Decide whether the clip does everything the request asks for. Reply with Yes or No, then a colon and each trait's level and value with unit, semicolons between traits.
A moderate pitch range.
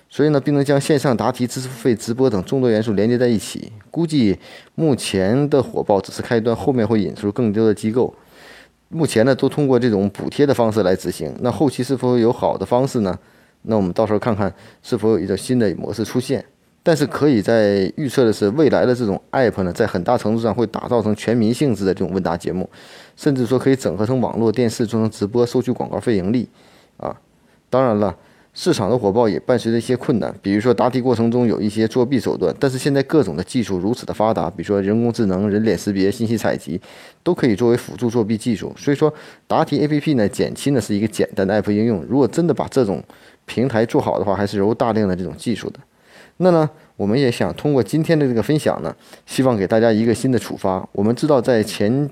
Yes: average, 3.8 semitones